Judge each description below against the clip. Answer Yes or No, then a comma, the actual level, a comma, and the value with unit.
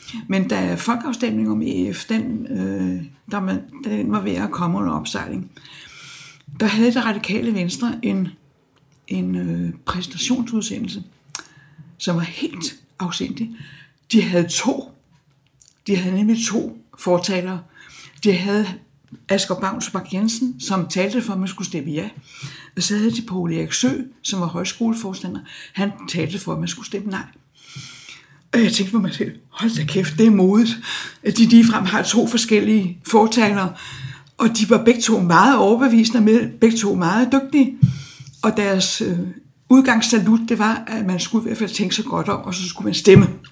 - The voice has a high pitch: Yes, high, 195 Hz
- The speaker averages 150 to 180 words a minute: Yes, average, 165 wpm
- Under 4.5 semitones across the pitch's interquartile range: No, average, 5.3 semitones